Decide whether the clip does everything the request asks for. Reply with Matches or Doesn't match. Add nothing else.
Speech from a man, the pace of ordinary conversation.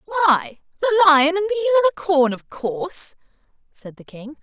Doesn't match